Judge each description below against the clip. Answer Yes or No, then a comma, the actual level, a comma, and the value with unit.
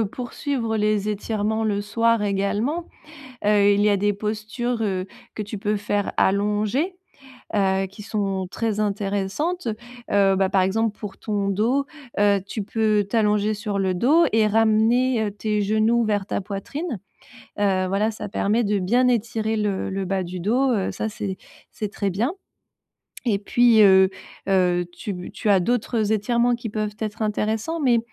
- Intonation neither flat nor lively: No, narrow, 2.2 semitones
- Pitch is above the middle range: Yes, high, 210 Hz